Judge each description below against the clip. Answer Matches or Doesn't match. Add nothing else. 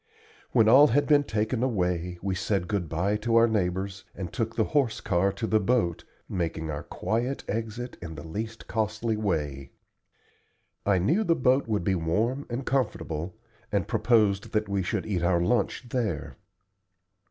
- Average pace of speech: Matches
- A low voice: Matches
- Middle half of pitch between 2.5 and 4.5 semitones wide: Doesn't match